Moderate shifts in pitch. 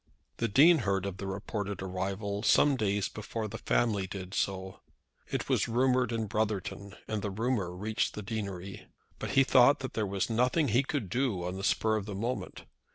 Yes: average, 3.5 semitones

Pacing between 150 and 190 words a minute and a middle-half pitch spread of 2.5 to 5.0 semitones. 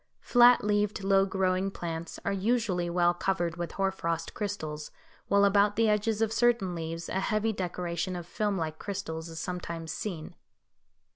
Yes: average, 160 wpm; average, 3.4 semitones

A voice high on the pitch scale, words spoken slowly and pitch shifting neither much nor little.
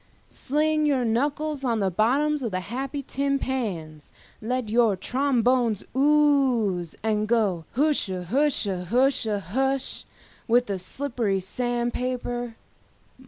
Yes: high, 245 Hz; slow, 110 wpm; average, 4.6 semitones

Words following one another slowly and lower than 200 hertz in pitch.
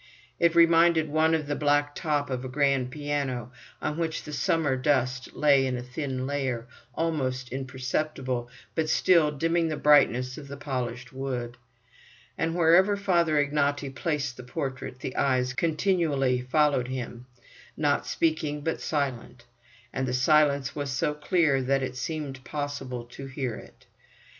No: average, 150 wpm; medium, 140 Hz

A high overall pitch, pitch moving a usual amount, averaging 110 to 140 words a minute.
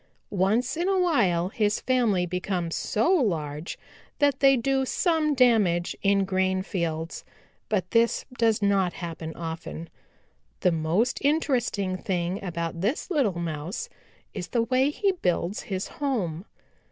No: high, 200 Hz; wide, 6.9 semitones; slow, 135 wpm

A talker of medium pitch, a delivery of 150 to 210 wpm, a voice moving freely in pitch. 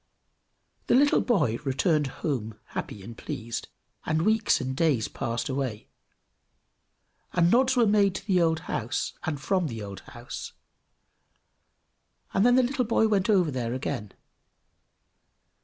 No: medium, 160 Hz; average, 140 wpm; wide, 8.8 semitones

